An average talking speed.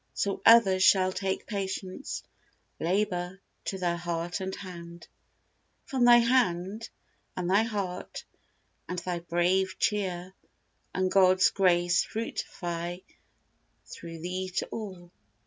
No: slow, 115 wpm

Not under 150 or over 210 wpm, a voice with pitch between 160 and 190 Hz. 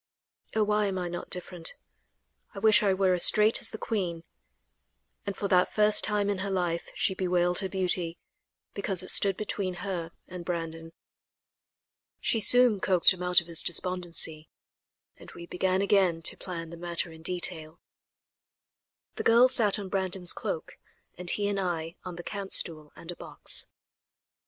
Yes: average, 170 wpm; medium, 185 Hz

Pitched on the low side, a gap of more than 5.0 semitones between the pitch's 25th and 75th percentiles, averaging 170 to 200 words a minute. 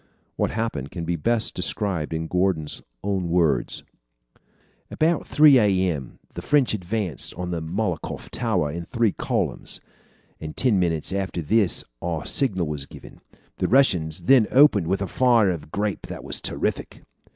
No: very low, 95 Hz; wide, 5.4 semitones; average, 155 wpm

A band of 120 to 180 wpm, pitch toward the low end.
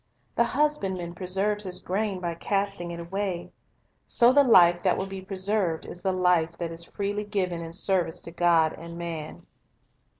No: average, 170 wpm; medium, 185 Hz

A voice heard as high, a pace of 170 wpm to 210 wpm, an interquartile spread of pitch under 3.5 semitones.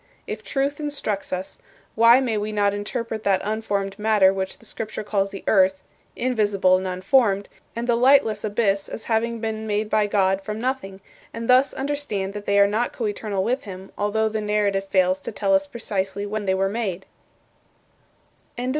Yes: high, 210 Hz; average, 175 wpm; average, 2.8 semitones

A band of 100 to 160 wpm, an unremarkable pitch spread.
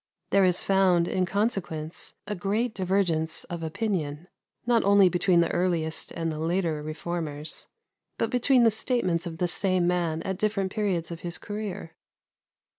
Yes: average, 155 wpm; average, 3.4 semitones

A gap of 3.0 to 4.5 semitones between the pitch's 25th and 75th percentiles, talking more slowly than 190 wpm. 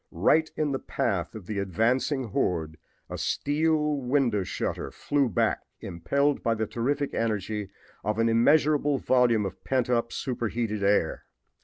No: average, 5.0 semitones; average, 145 wpm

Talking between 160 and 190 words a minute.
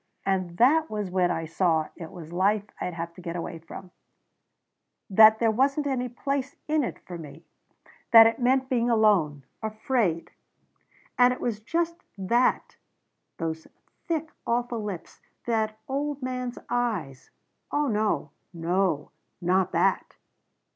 No: average, 140 wpm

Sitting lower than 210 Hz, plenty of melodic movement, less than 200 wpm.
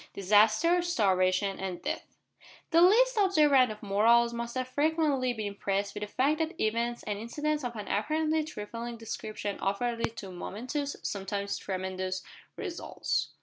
No: high, 235 Hz; wide, 6.8 semitones; average, 150 wpm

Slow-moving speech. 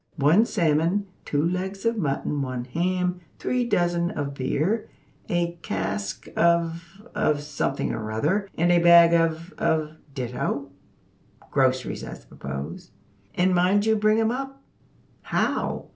Yes: slow, 130 wpm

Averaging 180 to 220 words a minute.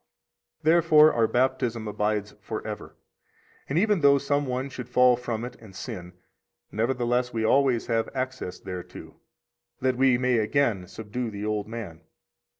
No: average, 150 wpm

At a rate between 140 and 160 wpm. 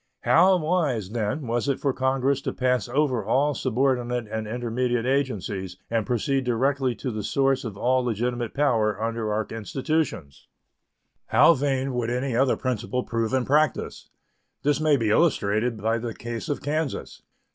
Yes: average, 155 wpm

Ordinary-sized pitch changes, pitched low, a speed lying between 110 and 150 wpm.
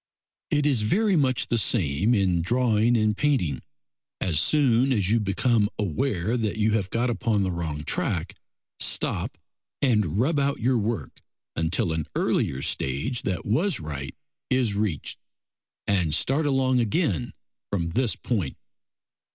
No: wide, 6.1 semitones; low, 110 Hz; average, 145 wpm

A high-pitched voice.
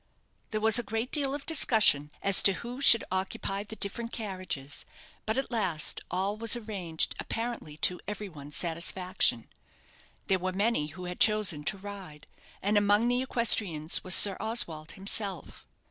Yes: high, 200 Hz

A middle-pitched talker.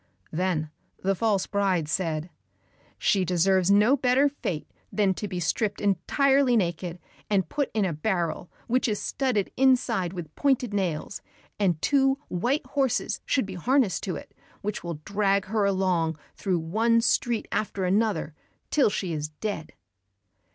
No: high, 195 Hz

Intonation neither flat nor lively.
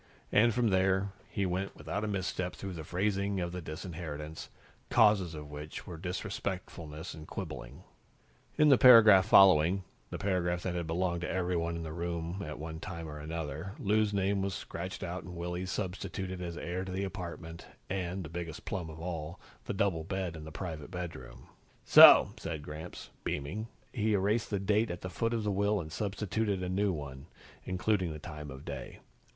Yes: average, 3.2 semitones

